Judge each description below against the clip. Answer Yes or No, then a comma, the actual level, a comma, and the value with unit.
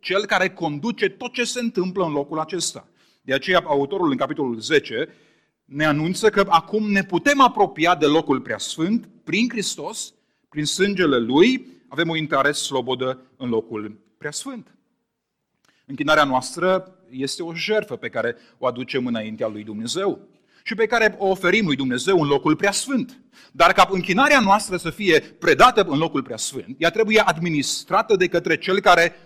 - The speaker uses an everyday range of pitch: No, wide, 6.2 semitones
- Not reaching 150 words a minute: No, average, 165 wpm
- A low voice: No, medium, 175 Hz